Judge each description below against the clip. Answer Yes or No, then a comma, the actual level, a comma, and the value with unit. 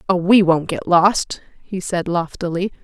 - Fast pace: No, average, 170 wpm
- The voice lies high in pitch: No, medium, 180 Hz